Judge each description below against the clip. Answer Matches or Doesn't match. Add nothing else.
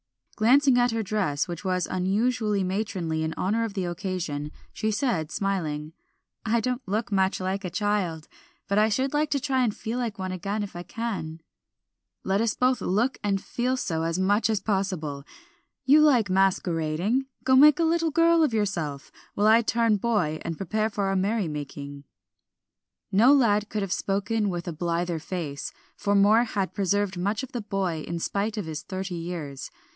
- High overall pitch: Matches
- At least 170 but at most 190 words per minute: Matches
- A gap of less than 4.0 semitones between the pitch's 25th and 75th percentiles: Doesn't match